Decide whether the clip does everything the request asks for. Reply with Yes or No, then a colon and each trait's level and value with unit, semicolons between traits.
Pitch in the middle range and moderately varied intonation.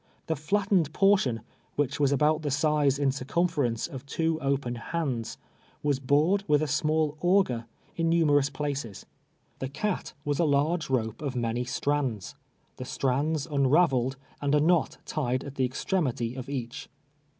Yes: medium, 145 Hz; average, 3.3 semitones